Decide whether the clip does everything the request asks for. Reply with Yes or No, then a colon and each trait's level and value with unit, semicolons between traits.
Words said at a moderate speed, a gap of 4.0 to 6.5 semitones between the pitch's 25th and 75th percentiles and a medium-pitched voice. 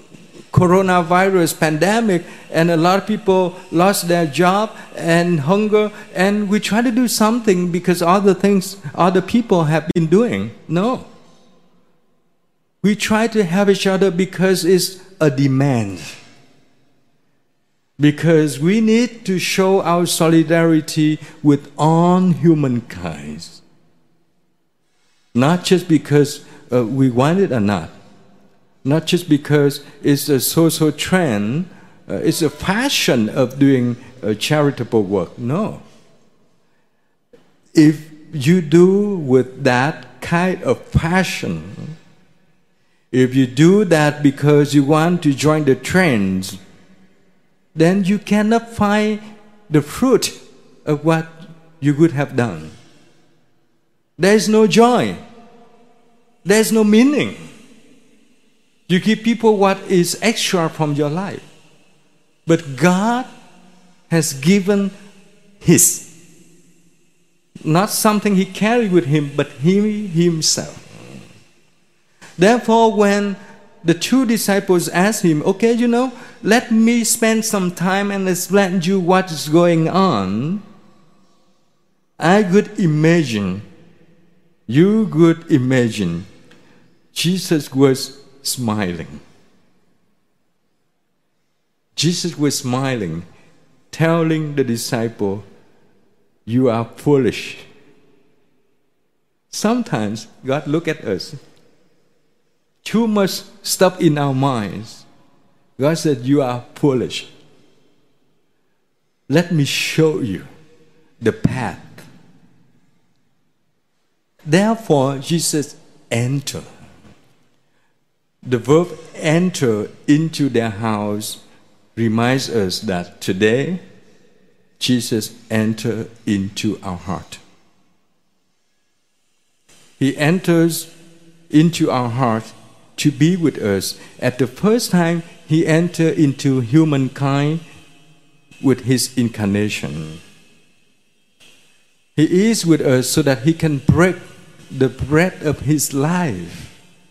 No: slow, 100 wpm; average, 5.2 semitones; medium, 165 Hz